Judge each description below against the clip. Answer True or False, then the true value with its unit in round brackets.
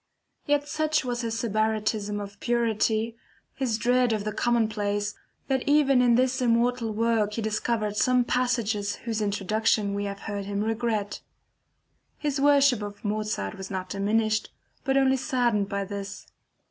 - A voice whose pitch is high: True (220 Hz)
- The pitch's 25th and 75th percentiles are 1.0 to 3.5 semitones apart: True (3.2 semitones)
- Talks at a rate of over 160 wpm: False (145 wpm)